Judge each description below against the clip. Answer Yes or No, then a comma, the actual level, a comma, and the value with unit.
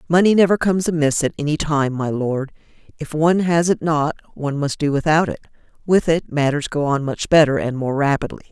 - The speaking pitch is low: No, medium, 155 Hz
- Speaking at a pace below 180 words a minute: No, fast, 205 wpm